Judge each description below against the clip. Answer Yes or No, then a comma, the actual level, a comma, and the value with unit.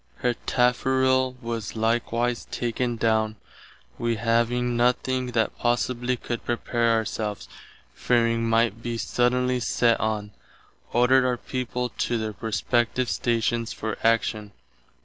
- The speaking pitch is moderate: No, low, 120 Hz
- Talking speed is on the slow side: Yes, slow, 120 wpm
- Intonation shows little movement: Yes, narrow, 1.4 semitones